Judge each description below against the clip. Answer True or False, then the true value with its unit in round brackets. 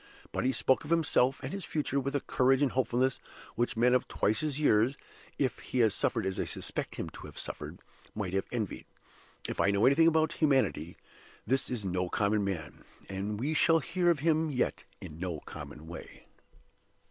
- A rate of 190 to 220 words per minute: True (195 wpm)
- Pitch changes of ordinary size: False (6.3 semitones)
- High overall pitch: False (125 Hz)